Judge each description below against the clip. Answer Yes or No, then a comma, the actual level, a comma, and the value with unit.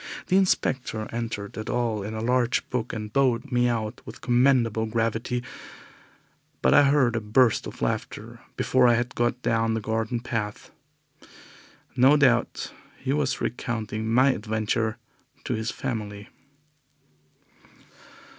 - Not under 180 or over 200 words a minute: No, slow, 135 wpm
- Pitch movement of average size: No, narrow, 2.3 semitones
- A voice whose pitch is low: Yes, low, 115 Hz